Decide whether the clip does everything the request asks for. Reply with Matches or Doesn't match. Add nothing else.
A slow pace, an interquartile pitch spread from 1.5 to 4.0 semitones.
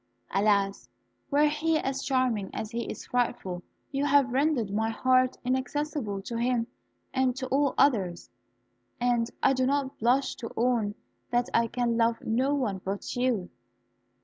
Doesn't match